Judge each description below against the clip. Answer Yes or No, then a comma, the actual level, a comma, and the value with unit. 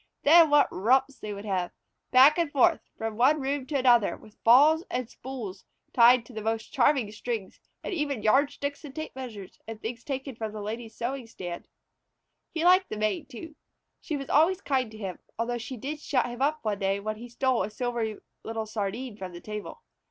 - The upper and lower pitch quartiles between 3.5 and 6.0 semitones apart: Yes, average, 4.5 semitones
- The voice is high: Yes, high, 240 Hz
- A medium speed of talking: Yes, average, 195 wpm